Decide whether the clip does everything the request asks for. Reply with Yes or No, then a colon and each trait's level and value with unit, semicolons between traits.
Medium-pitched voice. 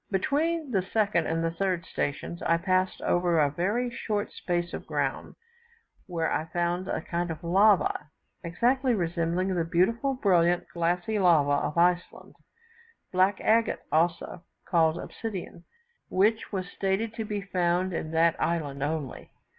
Yes: medium, 180 Hz